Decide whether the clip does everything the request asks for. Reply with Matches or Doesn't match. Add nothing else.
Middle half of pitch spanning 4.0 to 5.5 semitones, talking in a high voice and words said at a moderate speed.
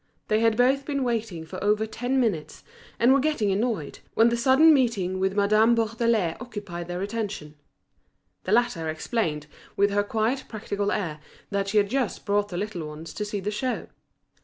Doesn't match